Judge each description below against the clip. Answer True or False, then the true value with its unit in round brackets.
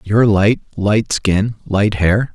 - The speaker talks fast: False (155 wpm)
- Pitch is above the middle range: False (105 Hz)